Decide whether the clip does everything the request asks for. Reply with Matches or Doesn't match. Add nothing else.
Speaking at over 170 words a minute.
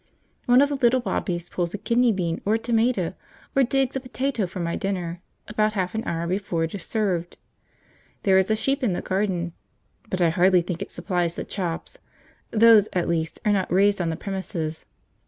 Matches